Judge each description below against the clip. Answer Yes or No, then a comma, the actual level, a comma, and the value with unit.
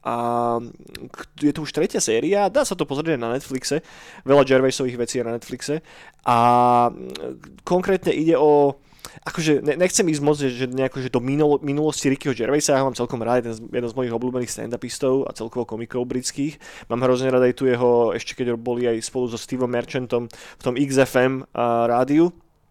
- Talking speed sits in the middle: No, fast, 175 wpm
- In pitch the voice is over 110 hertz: Yes, low, 130 Hz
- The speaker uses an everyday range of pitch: Yes, average, 3.2 semitones